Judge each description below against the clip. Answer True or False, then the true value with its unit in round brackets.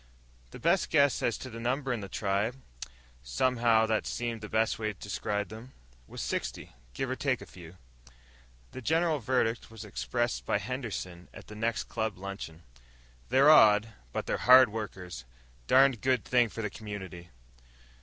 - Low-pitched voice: True (110 Hz)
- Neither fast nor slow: True (165 wpm)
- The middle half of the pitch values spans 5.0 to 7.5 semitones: False (4.2 semitones)